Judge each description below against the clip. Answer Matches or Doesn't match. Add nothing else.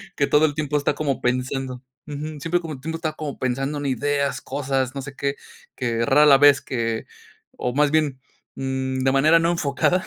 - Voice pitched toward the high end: Doesn't match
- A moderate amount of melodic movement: Doesn't match